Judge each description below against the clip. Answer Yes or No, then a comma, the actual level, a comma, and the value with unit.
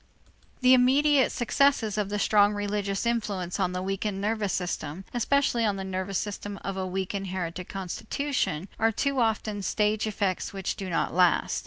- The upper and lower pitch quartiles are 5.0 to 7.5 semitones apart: No, average, 2.9 semitones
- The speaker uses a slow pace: No, average, 165 wpm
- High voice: Yes, high, 205 Hz